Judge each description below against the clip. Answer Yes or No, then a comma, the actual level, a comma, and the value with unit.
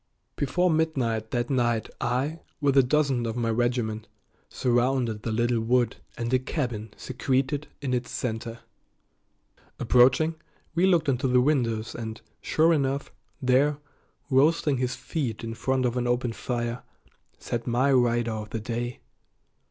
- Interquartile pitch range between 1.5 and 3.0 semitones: Yes, narrow, 2.6 semitones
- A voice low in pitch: Yes, low, 125 Hz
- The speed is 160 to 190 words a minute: No, average, 145 wpm